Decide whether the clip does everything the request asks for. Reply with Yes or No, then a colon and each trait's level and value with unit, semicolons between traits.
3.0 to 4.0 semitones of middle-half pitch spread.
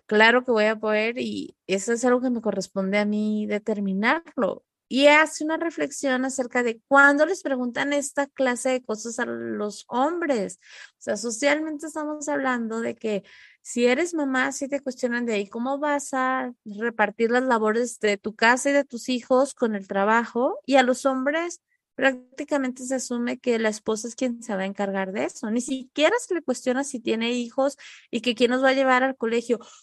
Yes: average, 3.7 semitones